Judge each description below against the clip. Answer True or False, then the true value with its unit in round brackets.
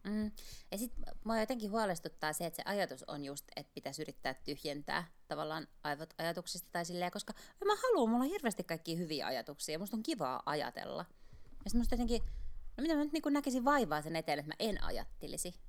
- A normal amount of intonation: False (6.7 semitones)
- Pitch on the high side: True (200 Hz)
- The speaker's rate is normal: False (200 wpm)